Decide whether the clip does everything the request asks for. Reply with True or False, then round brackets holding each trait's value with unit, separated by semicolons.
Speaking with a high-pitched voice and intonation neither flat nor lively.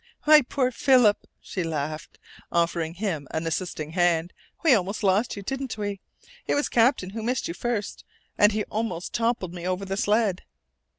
True (200 Hz; 4.9 semitones)